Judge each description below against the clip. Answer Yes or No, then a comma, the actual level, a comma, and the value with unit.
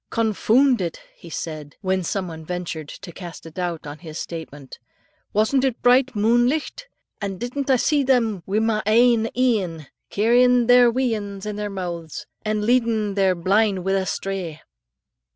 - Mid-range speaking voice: No, high, 210 Hz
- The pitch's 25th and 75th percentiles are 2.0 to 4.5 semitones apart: No, average, 5.2 semitones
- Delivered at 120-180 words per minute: Yes, average, 165 wpm